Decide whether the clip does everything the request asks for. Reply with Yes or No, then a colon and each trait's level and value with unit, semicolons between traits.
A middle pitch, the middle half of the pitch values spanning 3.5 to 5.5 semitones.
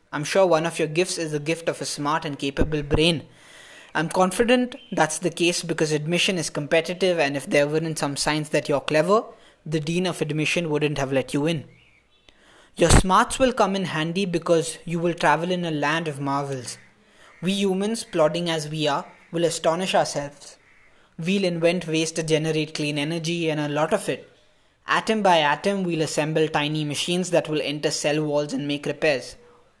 No: medium, 160 Hz; average, 2.7 semitones